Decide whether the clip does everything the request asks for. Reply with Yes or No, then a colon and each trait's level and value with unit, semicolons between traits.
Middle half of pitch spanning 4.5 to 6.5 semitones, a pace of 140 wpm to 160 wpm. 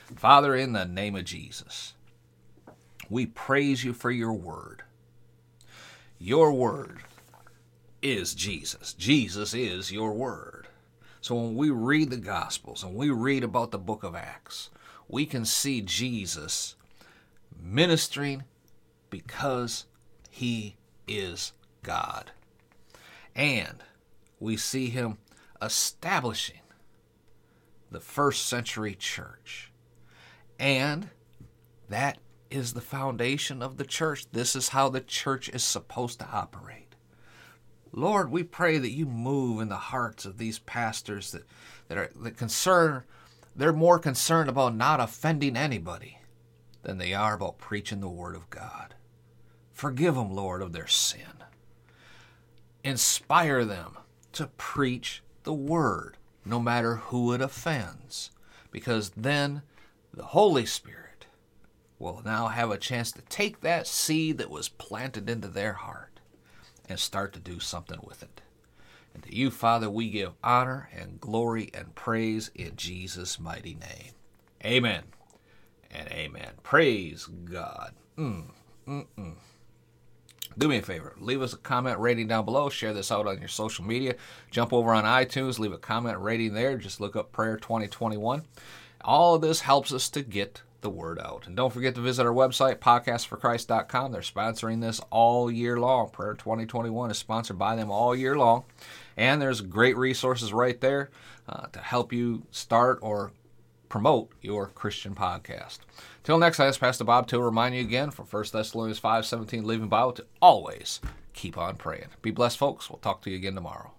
No: average, 3.1 semitones; average, 145 wpm